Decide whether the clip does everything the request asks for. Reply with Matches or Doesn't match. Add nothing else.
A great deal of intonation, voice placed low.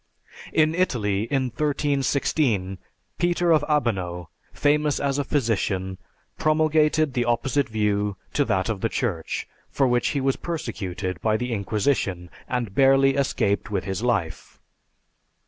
Matches